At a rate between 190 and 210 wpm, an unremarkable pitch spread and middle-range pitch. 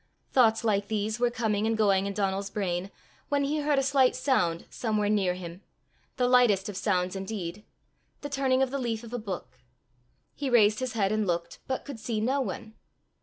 No: average, 195 wpm; average, 4.2 semitones; high, 215 Hz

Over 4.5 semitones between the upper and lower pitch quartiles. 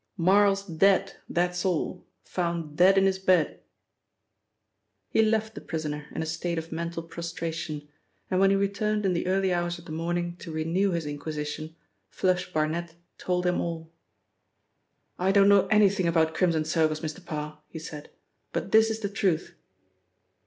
No: average, 3.2 semitones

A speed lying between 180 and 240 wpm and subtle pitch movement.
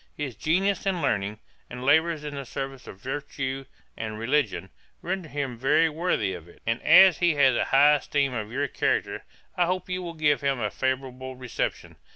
No: average, 190 wpm; average, 4.1 semitones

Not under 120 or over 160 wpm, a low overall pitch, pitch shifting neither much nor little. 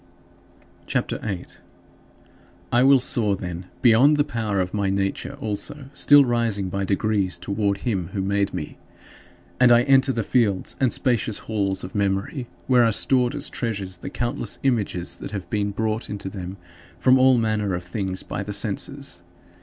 No: average, 170 wpm; low, 105 Hz; average, 3.8 semitones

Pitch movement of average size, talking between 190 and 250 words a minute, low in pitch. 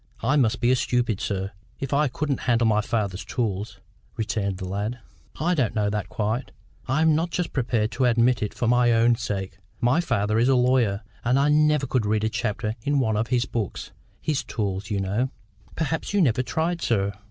Yes: average, 4.0 semitones; average, 200 wpm; low, 120 Hz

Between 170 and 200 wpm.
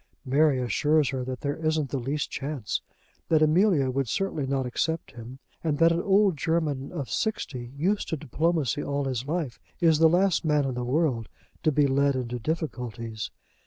Yes: average, 180 wpm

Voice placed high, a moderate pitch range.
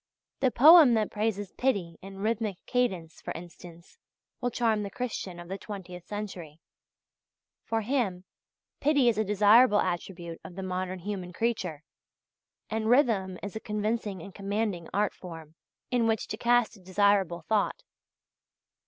Yes: high, 205 Hz; average, 3.7 semitones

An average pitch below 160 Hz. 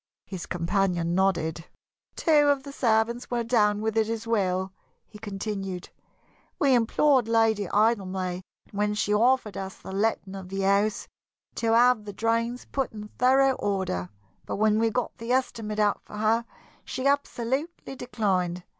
No: high, 215 Hz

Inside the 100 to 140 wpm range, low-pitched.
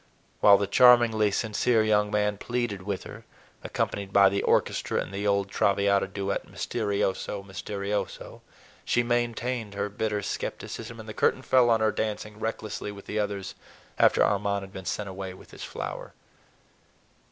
No: average, 150 wpm; low, 105 Hz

